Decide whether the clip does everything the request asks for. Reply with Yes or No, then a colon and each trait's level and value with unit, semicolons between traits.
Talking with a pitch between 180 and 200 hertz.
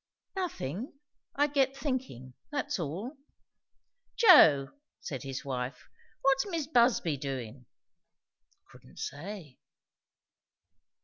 Yes: medium, 185 Hz